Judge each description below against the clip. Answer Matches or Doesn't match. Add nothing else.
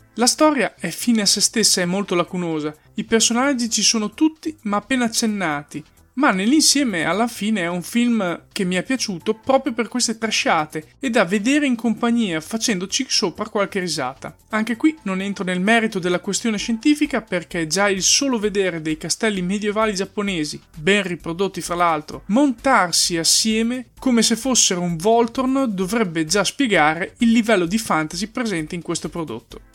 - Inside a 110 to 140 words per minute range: Doesn't match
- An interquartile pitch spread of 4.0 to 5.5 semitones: Matches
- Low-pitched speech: Doesn't match